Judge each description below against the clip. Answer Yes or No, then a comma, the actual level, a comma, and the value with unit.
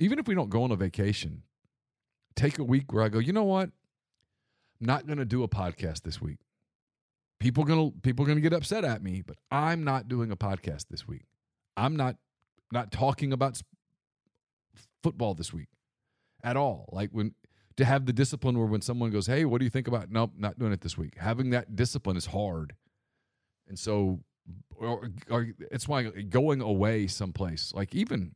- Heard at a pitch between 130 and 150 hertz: No, low, 120 Hz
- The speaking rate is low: No, fast, 205 wpm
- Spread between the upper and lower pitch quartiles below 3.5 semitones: No, average, 5.1 semitones